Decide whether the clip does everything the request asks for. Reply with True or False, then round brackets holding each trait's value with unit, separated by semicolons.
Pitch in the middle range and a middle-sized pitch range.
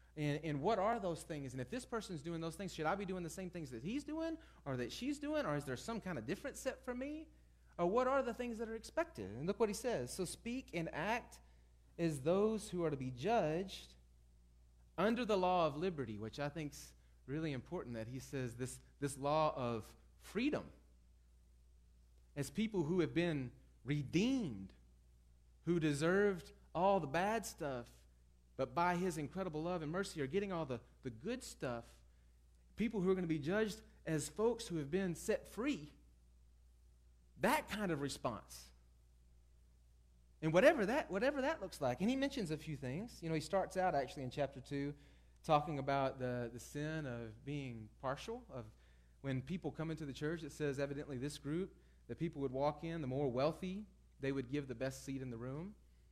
False (150 Hz; 7.9 semitones)